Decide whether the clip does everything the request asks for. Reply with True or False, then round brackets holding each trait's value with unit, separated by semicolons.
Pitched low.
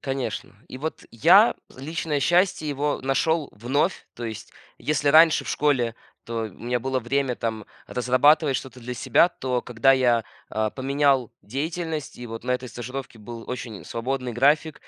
True (130 Hz)